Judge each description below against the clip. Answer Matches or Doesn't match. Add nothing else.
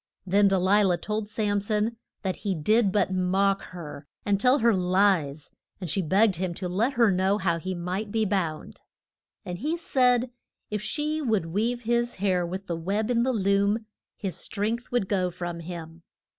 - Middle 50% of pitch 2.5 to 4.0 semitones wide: Matches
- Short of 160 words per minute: Doesn't match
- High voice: Matches